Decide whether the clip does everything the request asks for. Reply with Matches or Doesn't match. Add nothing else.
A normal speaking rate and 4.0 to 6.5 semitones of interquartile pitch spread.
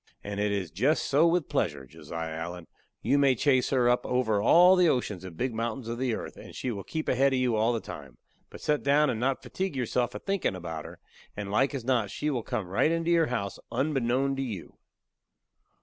Doesn't match